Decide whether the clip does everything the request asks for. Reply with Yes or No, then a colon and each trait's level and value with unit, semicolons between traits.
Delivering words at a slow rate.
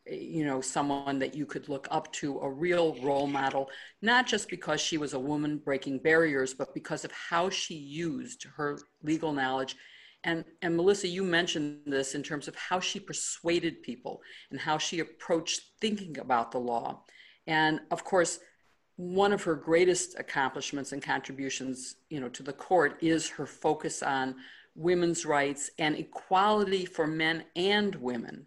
No: average, 165 wpm